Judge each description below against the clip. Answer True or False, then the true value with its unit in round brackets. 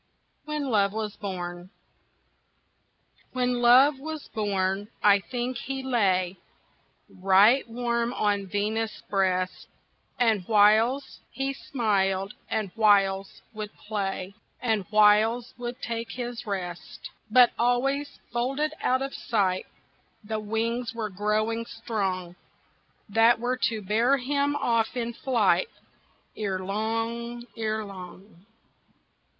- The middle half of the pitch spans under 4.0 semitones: True (3.5 semitones)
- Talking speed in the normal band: False (105 wpm)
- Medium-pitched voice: False (220 Hz)